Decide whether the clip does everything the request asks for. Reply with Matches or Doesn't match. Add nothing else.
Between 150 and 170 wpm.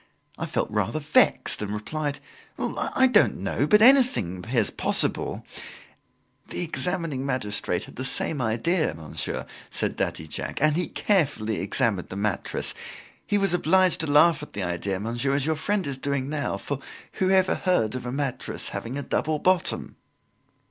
Matches